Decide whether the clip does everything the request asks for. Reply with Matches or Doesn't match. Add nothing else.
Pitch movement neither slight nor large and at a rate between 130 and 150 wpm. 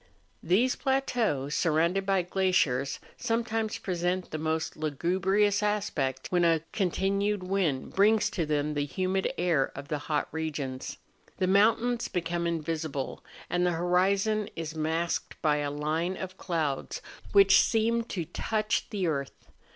Matches